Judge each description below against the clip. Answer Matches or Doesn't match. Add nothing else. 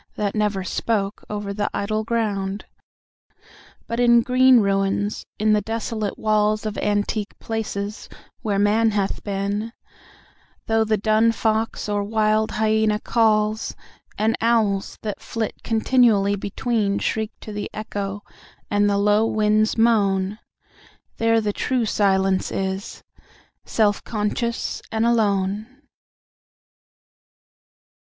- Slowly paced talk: Matches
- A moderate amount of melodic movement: Doesn't match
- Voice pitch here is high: Matches